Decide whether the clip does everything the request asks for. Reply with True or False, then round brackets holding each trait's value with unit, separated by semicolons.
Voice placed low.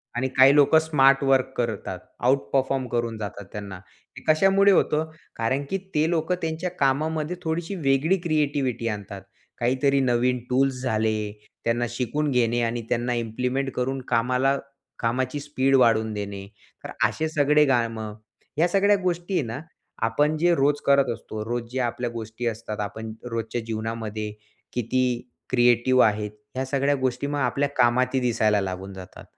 True (125 Hz)